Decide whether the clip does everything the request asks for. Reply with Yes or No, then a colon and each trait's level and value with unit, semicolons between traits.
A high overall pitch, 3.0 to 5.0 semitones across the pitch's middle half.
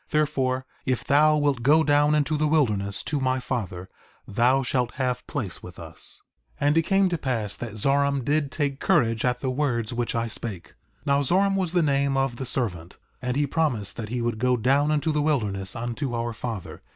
No: low, 130 Hz; average, 3.9 semitones